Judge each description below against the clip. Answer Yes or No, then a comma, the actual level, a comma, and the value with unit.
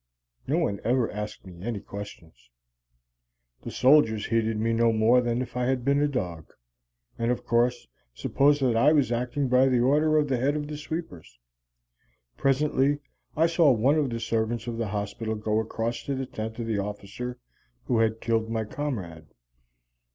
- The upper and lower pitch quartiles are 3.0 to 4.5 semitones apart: Yes, average, 3.5 semitones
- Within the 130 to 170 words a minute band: No, average, 180 wpm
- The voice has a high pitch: No, low, 120 Hz